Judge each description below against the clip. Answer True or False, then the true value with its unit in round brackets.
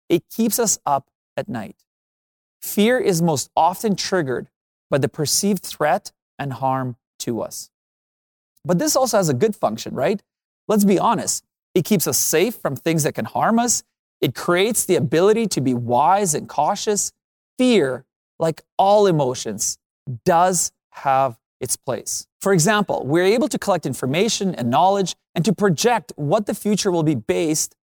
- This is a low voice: False (180 Hz)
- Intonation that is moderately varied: False (6.7 semitones)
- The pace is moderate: True (160 wpm)